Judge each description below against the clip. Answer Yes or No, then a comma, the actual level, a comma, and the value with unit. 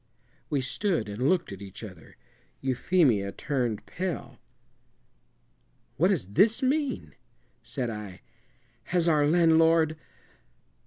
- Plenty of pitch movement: Yes, wide, 8.3 semitones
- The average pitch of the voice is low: No, medium, 150 Hz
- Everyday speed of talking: No, slow, 105 wpm